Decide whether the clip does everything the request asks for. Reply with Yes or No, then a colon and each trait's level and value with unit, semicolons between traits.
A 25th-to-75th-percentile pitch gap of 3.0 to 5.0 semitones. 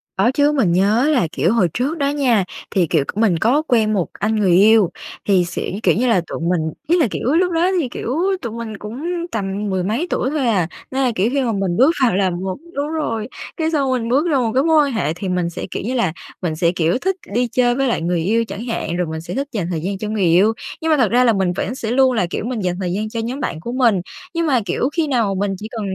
No: wide, 5.6 semitones